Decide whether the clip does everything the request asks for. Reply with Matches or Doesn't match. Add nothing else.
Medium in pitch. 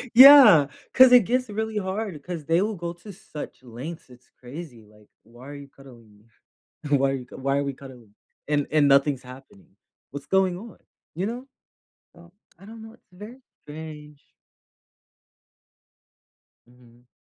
Matches